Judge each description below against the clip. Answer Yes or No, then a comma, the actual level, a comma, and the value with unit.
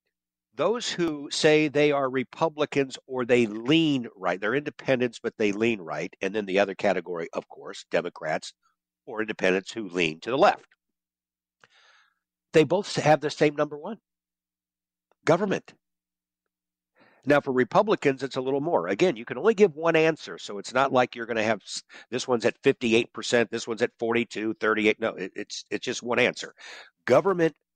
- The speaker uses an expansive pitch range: Yes, wide, 6.7 semitones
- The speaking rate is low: No, average, 165 wpm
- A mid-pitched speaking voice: No, low, 120 Hz